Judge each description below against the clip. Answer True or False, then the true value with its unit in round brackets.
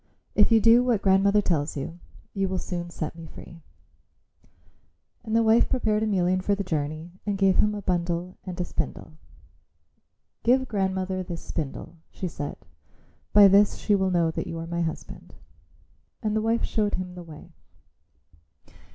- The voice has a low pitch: False (190 Hz)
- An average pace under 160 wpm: False (165 wpm)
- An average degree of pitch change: True (3.5 semitones)